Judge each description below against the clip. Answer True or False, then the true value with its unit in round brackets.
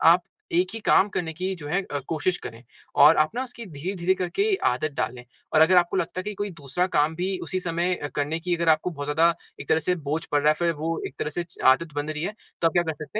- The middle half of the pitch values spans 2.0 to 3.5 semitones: True (3.2 semitones)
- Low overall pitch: False (165 Hz)